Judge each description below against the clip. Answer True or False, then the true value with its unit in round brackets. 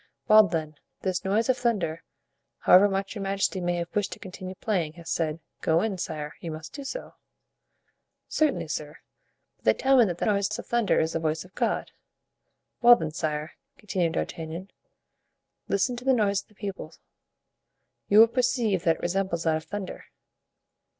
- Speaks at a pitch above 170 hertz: True (190 Hz)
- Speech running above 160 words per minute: True (175 wpm)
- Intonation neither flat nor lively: True (4.5 semitones)